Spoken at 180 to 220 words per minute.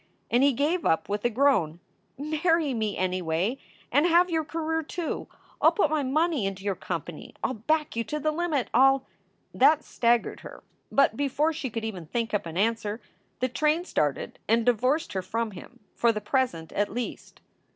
Yes: average, 195 wpm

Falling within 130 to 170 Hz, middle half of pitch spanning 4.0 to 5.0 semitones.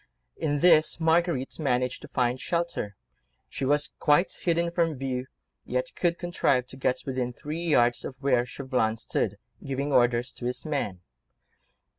Yes: medium, 140 Hz; average, 4.6 semitones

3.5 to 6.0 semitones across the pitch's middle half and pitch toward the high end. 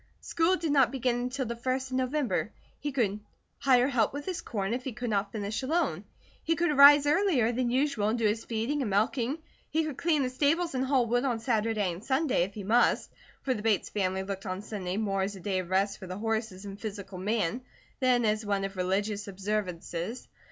Yes: average, 4.7 semitones; high, 230 Hz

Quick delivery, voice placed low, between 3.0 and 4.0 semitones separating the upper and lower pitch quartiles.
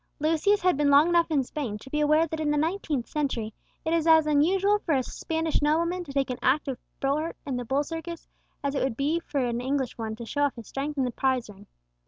No: fast, 245 wpm; very high, 290 Hz; average, 3.5 semitones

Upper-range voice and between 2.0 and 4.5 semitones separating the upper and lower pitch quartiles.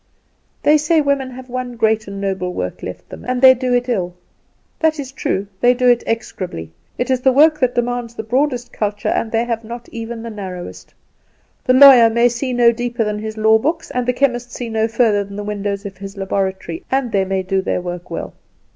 Yes: high, 235 Hz; average, 3.7 semitones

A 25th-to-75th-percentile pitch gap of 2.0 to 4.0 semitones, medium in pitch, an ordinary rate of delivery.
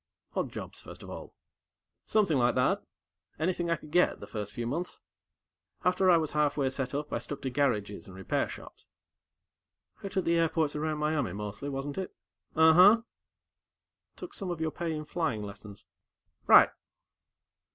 No: average, 5.0 semitones; medium, 150 Hz; average, 160 wpm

